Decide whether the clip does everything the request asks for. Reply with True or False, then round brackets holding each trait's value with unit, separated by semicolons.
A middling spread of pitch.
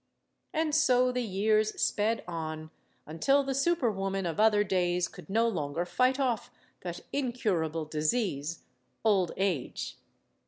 False (6.3 semitones)